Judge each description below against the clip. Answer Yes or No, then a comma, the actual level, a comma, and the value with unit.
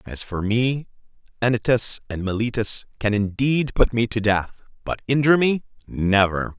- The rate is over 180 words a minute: No, average, 145 wpm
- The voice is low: Yes, low, 115 Hz